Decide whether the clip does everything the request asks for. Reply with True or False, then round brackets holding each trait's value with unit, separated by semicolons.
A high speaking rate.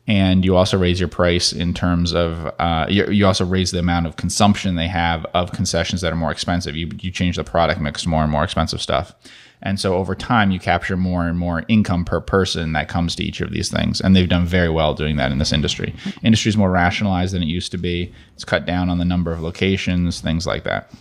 True (245 wpm)